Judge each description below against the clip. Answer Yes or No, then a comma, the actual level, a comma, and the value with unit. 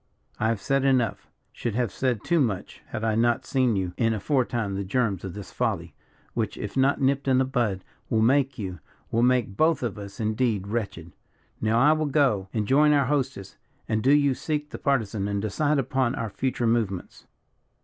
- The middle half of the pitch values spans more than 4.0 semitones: Yes, average, 4.4 semitones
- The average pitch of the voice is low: Yes, low, 120 Hz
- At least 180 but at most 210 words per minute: Yes, average, 195 wpm